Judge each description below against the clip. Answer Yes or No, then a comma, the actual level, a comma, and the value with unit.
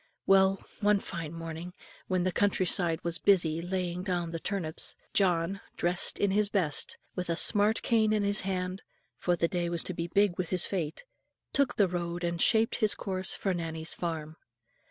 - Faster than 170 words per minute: Yes, average, 185 wpm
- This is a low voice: No, medium, 180 Hz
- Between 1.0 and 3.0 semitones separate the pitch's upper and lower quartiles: Yes, average, 2.7 semitones